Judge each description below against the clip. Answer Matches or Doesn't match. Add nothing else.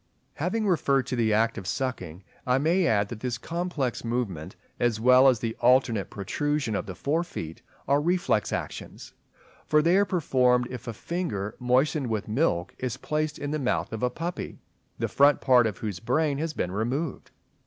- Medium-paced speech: Matches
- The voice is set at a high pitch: Doesn't match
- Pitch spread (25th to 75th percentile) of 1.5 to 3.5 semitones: Doesn't match